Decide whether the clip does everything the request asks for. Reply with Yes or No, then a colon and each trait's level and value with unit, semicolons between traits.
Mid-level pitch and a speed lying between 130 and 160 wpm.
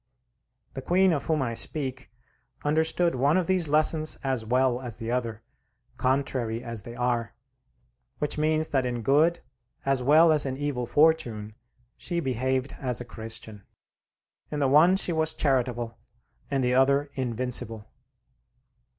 No: low, 130 Hz; average, 145 wpm